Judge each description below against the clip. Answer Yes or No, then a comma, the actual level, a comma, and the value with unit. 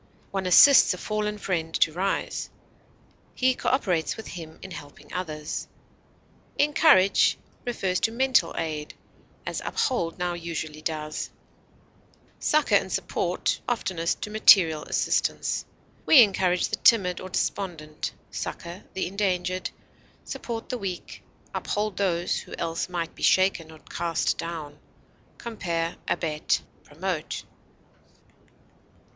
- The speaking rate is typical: No, slow, 115 wpm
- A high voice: No, medium, 180 Hz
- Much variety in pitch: No, average, 4.0 semitones